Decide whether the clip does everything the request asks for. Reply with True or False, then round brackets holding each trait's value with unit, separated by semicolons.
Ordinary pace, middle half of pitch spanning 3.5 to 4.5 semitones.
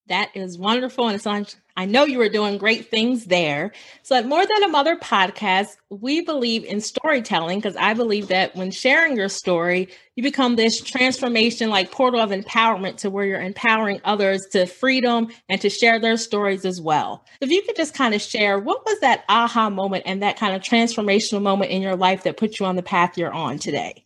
False (210 wpm; 3.9 semitones)